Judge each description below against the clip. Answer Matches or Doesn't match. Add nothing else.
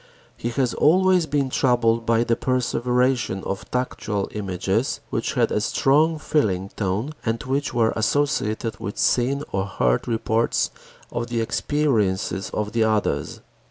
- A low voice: Matches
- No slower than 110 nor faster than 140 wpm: Matches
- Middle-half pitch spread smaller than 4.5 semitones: Matches